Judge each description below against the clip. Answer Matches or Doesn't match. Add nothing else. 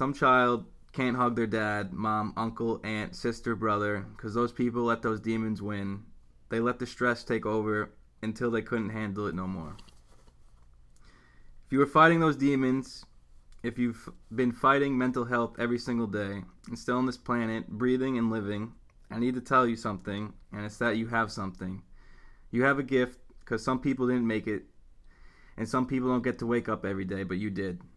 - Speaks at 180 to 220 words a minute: Matches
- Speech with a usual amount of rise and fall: Matches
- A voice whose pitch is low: Matches